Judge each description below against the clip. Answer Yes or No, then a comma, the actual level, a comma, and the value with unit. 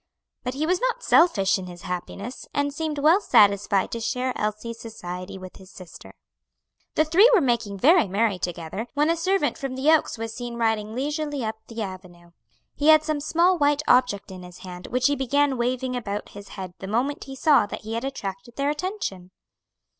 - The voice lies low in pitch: No, high, 240 Hz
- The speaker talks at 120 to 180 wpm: No, average, 195 wpm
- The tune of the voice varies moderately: No, wide, 6.7 semitones